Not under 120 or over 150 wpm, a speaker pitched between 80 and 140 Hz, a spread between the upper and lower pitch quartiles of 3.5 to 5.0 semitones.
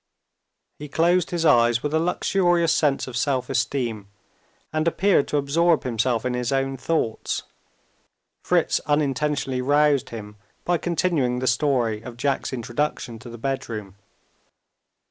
Yes: slow, 135 wpm; low, 135 Hz; average, 4.5 semitones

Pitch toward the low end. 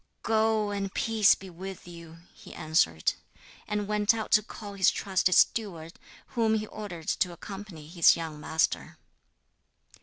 No: high, 195 Hz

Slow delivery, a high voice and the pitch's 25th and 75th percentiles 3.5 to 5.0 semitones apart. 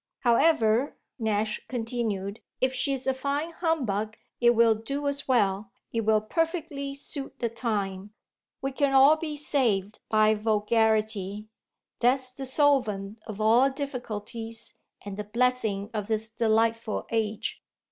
Yes: slow, 130 wpm; high, 230 Hz; average, 4.0 semitones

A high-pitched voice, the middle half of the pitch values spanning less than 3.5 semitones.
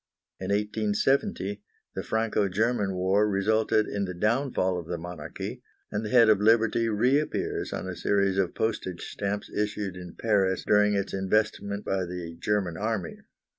No: low, 105 Hz; narrow, 2.5 semitones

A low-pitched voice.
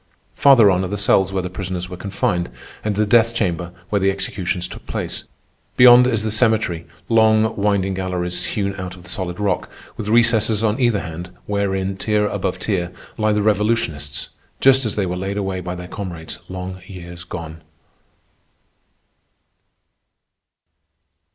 Yes: very low, 95 Hz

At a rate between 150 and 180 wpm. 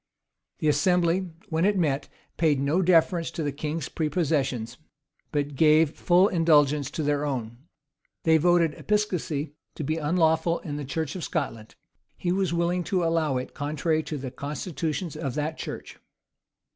Yes: average, 155 wpm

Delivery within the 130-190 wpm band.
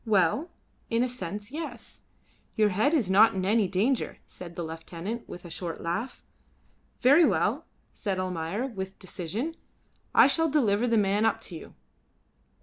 Yes: average, 155 wpm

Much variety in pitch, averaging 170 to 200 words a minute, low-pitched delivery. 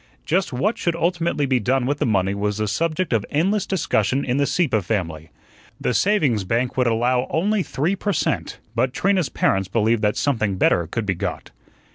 Yes: wide, 7.8 semitones; average, 190 wpm; low, 125 Hz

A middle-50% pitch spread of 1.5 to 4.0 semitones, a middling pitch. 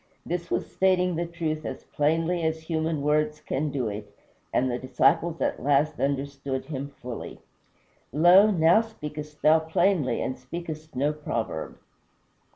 Yes: average, 3.4 semitones; medium, 155 Hz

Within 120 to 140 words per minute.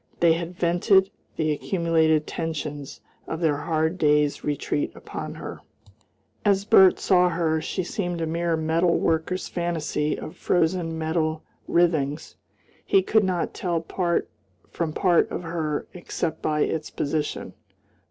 Yes: slow, 135 wpm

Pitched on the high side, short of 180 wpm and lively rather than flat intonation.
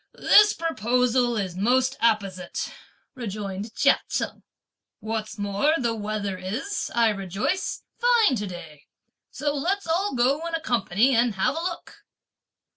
Yes: high, 235 Hz; slow, 135 wpm; wide, 6.3 semitones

